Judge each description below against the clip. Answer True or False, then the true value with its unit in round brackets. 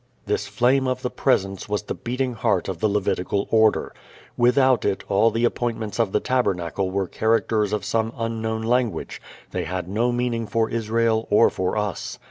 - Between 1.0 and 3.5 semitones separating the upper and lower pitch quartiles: True (2.9 semitones)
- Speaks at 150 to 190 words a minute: True (175 wpm)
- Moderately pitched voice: False (110 Hz)